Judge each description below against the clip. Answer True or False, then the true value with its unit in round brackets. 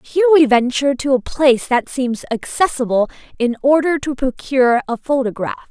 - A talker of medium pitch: False (265 Hz)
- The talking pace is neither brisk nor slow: True (160 wpm)